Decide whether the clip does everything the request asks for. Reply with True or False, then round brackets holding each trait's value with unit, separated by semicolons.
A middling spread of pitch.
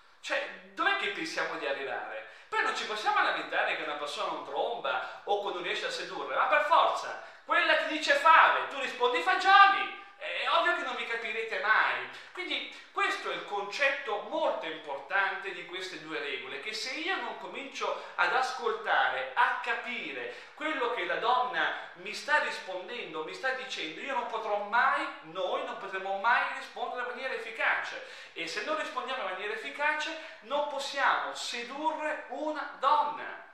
False (5.9 semitones)